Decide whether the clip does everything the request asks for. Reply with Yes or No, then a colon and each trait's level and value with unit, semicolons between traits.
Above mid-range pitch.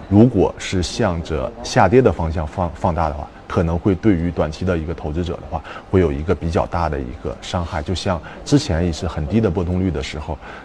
No: very low, 85 Hz